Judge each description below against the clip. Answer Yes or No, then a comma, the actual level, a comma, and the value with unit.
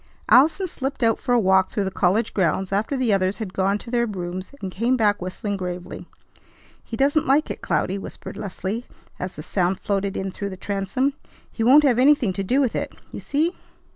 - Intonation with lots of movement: No, average, 5.0 semitones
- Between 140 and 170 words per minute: No, fast, 205 wpm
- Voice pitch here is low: No, high, 205 Hz